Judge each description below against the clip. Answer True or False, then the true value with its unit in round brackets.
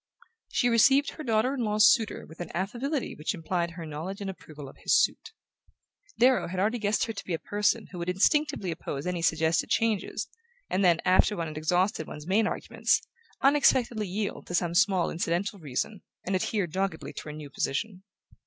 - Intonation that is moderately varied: True (4.5 semitones)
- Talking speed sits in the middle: True (190 wpm)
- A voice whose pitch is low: False (190 Hz)